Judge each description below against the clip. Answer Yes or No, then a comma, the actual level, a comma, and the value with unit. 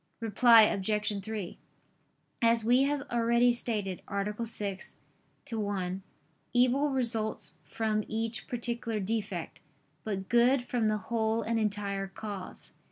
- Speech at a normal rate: No, slow, 120 wpm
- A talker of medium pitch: No, high, 220 Hz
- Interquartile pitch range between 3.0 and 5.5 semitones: No, narrow, 2.6 semitones